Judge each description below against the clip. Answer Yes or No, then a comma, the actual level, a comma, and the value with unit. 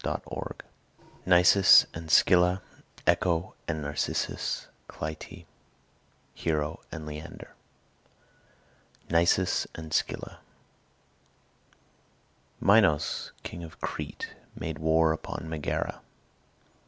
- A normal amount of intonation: No, narrow, 2.2 semitones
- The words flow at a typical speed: No, slow, 80 wpm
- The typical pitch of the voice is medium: No, very low, 80 Hz